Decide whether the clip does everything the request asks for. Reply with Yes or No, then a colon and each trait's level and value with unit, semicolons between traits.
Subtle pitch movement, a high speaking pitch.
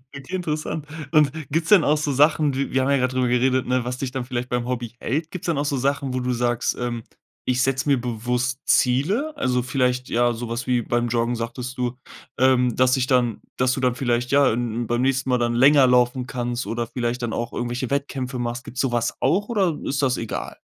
No: narrow, 2.2 semitones; low, 125 Hz